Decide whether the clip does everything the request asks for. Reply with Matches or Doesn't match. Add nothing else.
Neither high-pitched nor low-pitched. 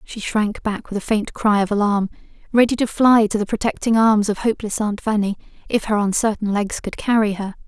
Doesn't match